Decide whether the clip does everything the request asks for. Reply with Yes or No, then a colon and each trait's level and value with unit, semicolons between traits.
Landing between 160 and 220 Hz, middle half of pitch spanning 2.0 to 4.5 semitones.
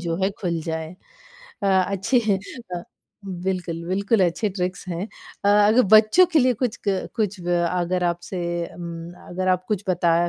Yes: medium, 185 Hz; average, 2.9 semitones